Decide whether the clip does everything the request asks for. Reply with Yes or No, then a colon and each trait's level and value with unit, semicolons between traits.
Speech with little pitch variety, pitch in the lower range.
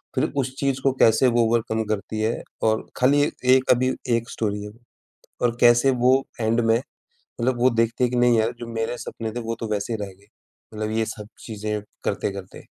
Yes: narrow, 2.0 semitones; low, 115 Hz